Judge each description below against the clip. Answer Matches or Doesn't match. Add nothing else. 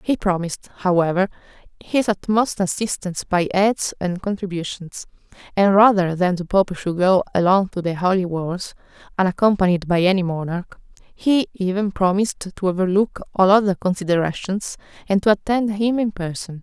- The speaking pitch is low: Doesn't match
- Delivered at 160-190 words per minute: Doesn't match